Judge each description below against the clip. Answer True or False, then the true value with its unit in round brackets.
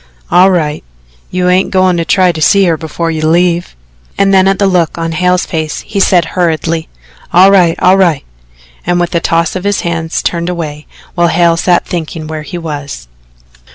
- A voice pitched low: False (170 Hz)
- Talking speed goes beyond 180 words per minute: True (190 wpm)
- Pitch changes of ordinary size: False (2.0 semitones)